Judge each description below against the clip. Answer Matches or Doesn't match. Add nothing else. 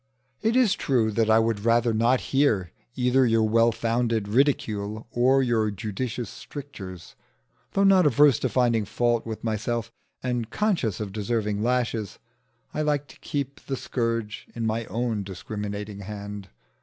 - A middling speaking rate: Matches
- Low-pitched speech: Matches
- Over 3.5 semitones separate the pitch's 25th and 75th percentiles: Doesn't match